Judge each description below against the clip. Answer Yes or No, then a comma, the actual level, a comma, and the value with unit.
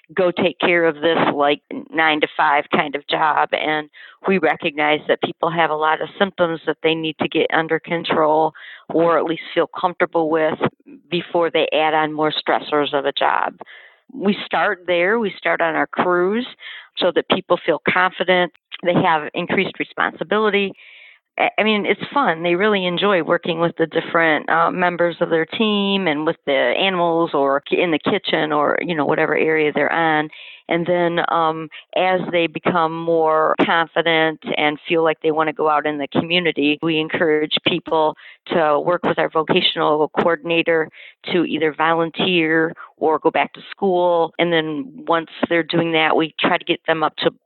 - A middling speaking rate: Yes, average, 180 wpm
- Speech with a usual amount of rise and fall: No, narrow, 2.1 semitones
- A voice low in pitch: No, medium, 165 Hz